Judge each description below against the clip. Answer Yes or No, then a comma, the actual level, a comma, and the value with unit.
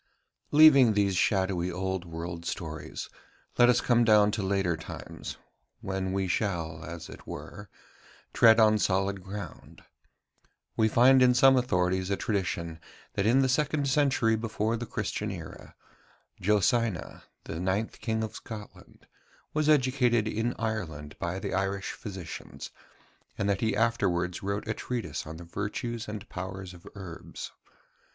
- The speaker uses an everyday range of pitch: Yes, average, 4.1 semitones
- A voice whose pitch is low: Yes, low, 100 Hz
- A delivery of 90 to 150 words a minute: Yes, average, 145 wpm